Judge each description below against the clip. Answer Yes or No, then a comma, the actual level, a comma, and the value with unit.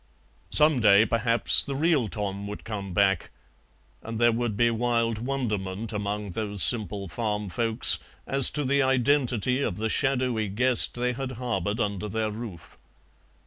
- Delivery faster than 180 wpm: No, average, 150 wpm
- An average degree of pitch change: Yes, average, 3.3 semitones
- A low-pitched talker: Yes, low, 115 Hz